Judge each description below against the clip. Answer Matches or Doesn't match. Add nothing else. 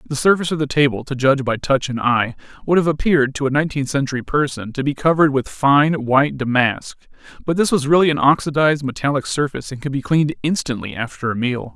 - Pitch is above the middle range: Doesn't match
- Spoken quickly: Matches